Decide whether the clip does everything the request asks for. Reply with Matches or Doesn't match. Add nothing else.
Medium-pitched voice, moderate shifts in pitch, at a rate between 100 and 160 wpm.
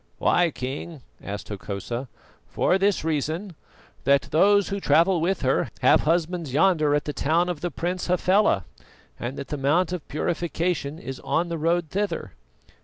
Matches